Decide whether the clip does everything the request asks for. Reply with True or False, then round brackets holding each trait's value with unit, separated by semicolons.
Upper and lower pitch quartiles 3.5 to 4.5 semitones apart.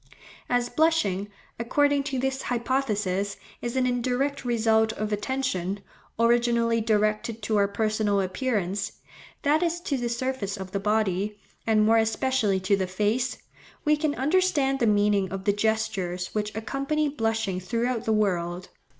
True (4.2 semitones)